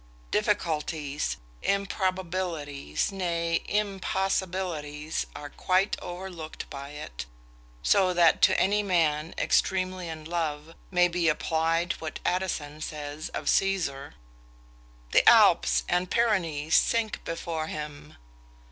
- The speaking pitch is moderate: Yes, medium, 165 Hz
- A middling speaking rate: No, slow, 105 wpm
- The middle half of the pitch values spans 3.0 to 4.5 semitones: Yes, average, 3.7 semitones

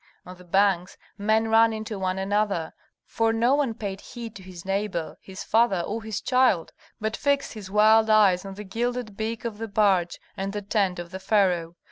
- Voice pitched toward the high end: Yes, high, 205 Hz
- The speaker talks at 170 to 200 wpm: Yes, average, 195 wpm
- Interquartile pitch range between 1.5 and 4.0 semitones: Yes, average, 2.8 semitones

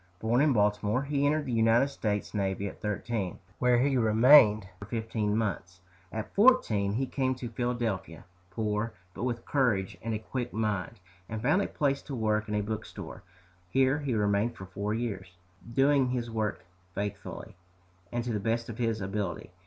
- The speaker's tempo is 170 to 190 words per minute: Yes, average, 175 wpm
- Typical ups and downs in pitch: Yes, average, 3.2 semitones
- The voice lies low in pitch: Yes, low, 110 Hz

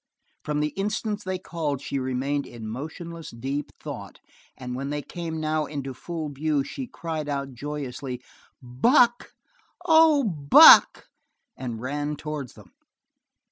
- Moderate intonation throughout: Yes, average, 3.8 semitones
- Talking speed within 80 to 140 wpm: Yes, slow, 135 wpm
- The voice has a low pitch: No, medium, 145 Hz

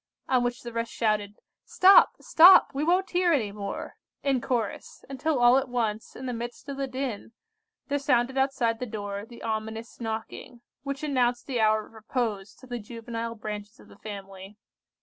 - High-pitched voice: Yes, high, 240 Hz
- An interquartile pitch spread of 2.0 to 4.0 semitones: Yes, average, 3.6 semitones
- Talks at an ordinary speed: Yes, average, 180 wpm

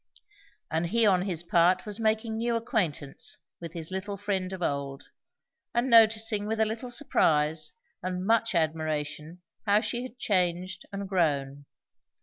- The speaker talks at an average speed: Yes, average, 145 wpm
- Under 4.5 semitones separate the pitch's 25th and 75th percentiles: No, average, 5.3 semitones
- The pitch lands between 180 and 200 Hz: Yes, medium, 185 Hz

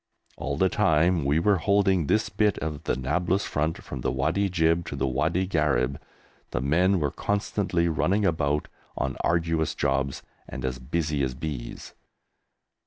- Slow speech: No, average, 160 wpm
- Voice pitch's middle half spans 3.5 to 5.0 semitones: Yes, average, 4.7 semitones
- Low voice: Yes, very low, 80 Hz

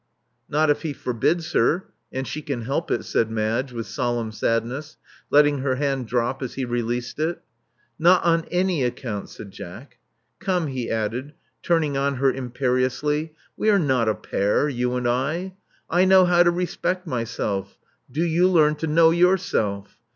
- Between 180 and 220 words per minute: No, average, 170 wpm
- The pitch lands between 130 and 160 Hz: Yes, medium, 140 Hz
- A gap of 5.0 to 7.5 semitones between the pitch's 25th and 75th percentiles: Yes, wide, 5.4 semitones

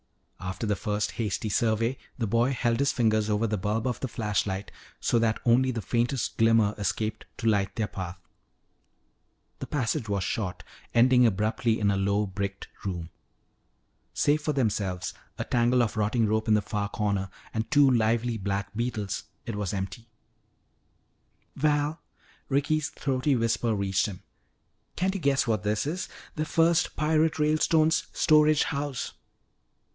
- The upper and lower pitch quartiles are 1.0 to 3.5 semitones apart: No, average, 4.5 semitones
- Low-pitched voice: Yes, low, 115 Hz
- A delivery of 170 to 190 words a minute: No, average, 150 wpm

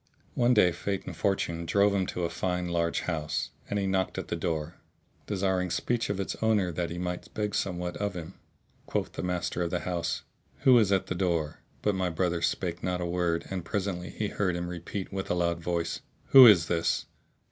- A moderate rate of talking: No, fast, 210 wpm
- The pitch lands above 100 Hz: No, very low, 90 Hz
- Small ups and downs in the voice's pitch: Yes, narrow, 2.3 semitones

